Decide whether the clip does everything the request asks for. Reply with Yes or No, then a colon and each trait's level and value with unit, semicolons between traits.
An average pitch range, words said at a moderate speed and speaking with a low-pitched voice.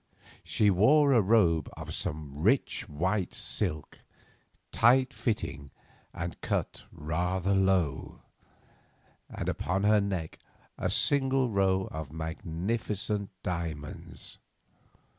No: average, 4.9 semitones; slow, 100 wpm; very low, 95 Hz